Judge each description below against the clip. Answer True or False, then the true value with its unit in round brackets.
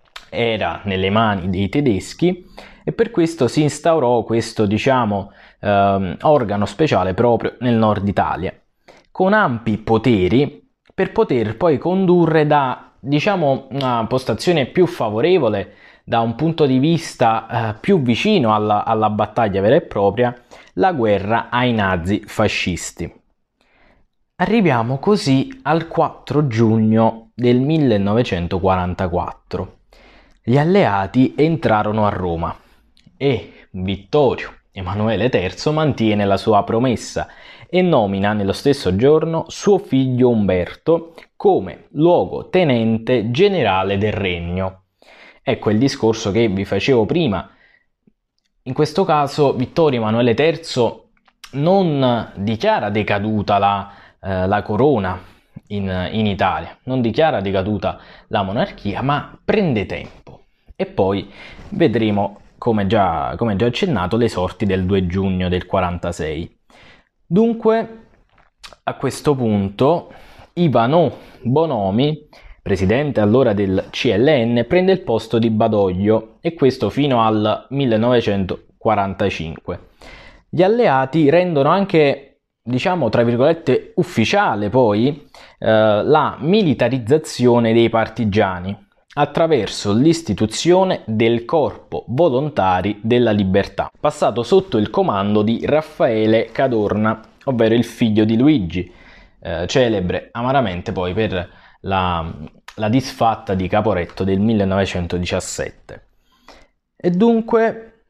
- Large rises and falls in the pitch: True (6.5 semitones)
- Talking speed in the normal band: False (110 wpm)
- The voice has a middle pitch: False (115 Hz)